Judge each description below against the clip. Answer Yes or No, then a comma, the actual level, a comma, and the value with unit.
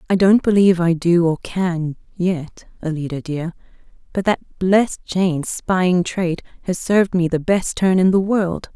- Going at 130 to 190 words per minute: Yes, average, 170 wpm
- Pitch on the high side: No, medium, 180 Hz